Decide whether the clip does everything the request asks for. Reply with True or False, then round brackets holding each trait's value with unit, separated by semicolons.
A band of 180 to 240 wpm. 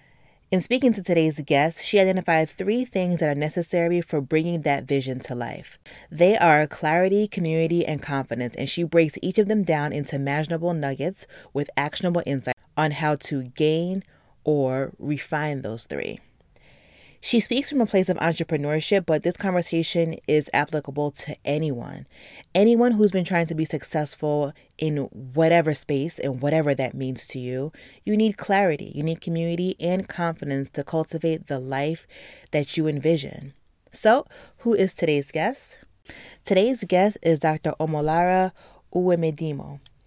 False (150 wpm)